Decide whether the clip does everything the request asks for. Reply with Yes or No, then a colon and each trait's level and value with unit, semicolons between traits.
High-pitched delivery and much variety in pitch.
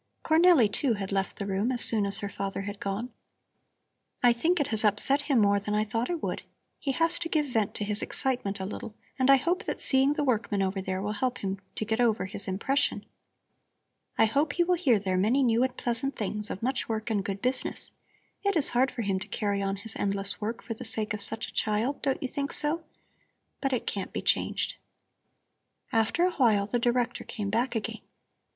No: high, 225 Hz; average, 4.8 semitones